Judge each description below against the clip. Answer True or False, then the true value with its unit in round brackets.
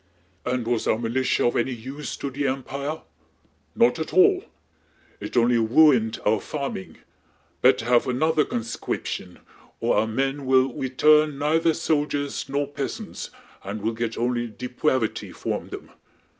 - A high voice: False (130 Hz)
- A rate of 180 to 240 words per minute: False (140 wpm)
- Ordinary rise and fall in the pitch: True (3.7 semitones)